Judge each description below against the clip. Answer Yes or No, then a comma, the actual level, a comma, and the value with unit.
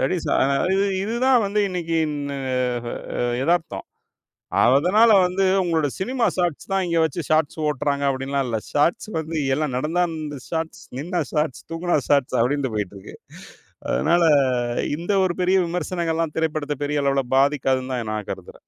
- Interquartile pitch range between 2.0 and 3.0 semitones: No, average, 4.0 semitones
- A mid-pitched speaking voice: Yes, medium, 155 Hz